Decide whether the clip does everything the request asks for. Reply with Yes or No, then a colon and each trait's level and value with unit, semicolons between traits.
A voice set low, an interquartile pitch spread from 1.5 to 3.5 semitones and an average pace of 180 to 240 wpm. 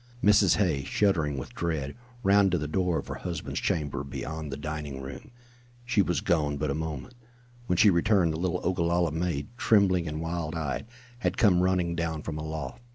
Yes: very low, 85 Hz; average, 3.2 semitones; average, 185 wpm